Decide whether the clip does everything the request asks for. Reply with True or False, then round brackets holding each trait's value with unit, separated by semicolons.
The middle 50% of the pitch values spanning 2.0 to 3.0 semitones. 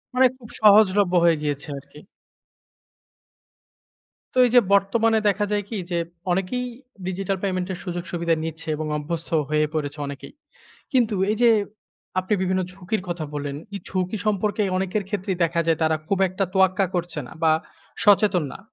False (3.7 semitones)